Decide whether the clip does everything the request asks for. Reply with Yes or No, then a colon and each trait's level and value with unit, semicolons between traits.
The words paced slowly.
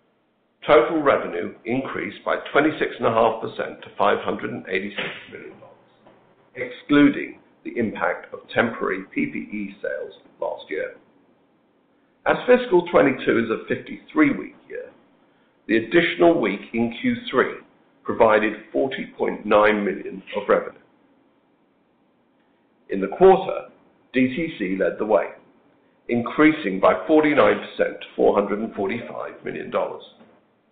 Yes: slow, 90 wpm